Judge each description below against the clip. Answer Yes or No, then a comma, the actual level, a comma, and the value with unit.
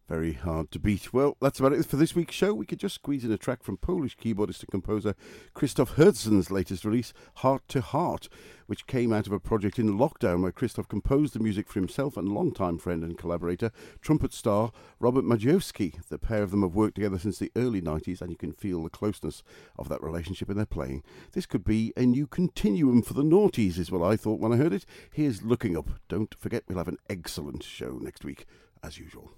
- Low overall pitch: Yes, low, 105 Hz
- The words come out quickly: Yes, fast, 225 wpm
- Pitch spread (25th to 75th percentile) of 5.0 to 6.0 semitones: Yes, wide, 5.4 semitones